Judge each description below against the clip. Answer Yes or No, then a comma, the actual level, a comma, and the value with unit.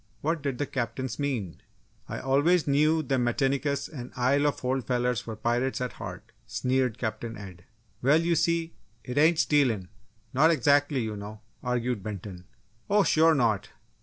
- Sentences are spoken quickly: No, average, 160 wpm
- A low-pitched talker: Yes, low, 130 Hz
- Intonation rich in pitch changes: No, average, 3.8 semitones